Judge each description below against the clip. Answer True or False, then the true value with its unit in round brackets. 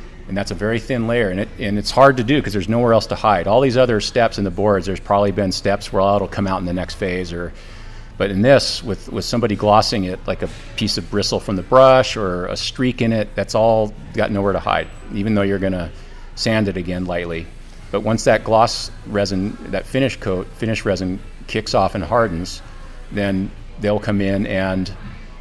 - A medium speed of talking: False (220 wpm)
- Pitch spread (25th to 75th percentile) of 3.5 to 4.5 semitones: False (2.8 semitones)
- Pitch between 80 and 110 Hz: True (100 Hz)